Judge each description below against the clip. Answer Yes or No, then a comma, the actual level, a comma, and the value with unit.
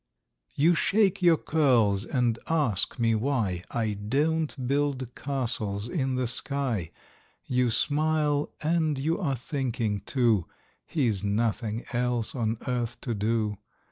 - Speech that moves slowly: Yes, slow, 125 wpm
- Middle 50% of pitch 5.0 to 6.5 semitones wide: No, average, 4.6 semitones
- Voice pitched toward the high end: No, low, 125 Hz